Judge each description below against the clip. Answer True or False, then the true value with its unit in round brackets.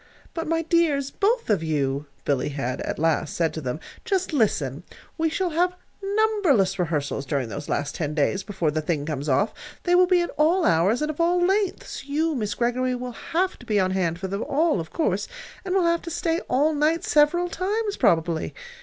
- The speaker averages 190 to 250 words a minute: True (205 wpm)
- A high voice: True (255 Hz)